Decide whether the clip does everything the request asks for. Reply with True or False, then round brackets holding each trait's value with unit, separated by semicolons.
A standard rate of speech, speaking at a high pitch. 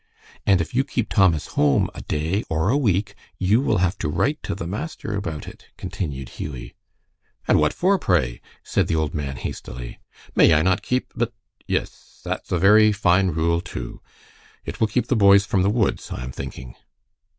False (190 wpm; 95 Hz)